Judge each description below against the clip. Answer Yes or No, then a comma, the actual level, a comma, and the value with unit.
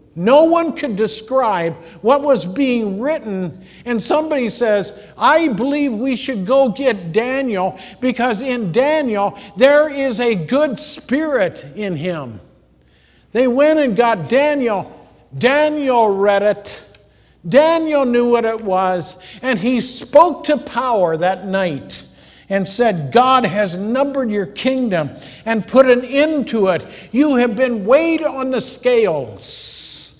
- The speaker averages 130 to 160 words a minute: Yes, slow, 135 wpm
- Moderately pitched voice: No, high, 245 Hz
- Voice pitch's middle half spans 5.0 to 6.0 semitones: Yes, wide, 5.4 semitones